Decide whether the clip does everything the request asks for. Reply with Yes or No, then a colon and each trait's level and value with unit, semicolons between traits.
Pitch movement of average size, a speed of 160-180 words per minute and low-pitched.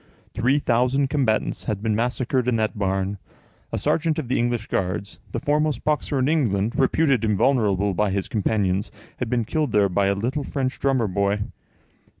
Yes: average, 4.9 semitones; average, 170 wpm; low, 115 Hz